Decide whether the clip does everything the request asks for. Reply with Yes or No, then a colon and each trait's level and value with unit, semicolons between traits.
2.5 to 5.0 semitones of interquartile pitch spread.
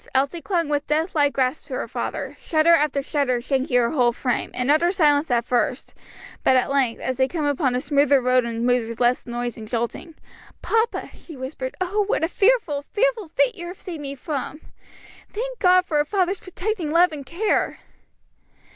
No: wide, 5.5 semitones